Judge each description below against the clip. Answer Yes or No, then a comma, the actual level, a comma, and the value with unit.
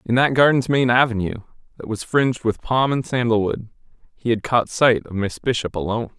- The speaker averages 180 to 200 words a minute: Yes, average, 195 wpm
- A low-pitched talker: Yes, low, 120 Hz